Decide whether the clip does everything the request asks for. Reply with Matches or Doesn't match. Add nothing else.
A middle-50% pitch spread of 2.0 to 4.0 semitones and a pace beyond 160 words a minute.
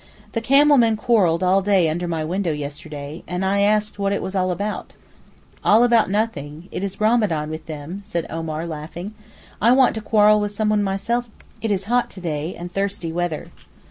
Doesn't match